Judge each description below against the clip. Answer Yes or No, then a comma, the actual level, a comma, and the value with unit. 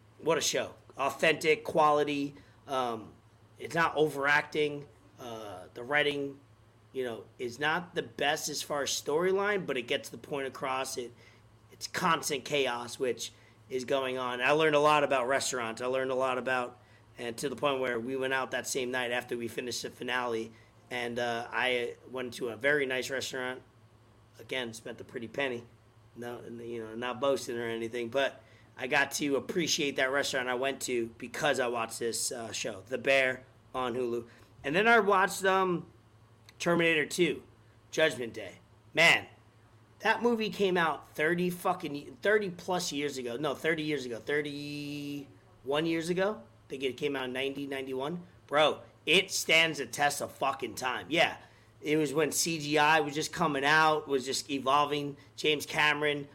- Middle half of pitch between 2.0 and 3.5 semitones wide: No, average, 4.0 semitones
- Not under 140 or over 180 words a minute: Yes, average, 170 wpm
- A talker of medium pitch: No, low, 130 Hz